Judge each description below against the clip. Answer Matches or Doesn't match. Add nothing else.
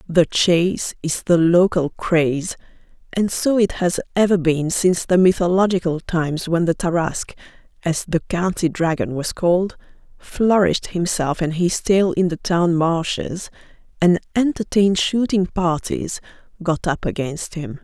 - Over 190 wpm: Doesn't match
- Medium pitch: Matches